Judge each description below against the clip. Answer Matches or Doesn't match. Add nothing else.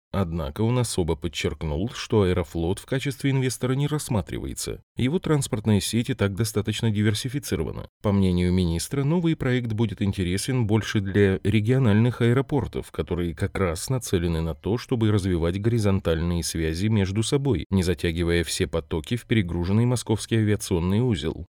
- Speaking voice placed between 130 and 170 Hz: Doesn't match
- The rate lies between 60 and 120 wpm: Doesn't match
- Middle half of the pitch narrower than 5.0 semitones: Doesn't match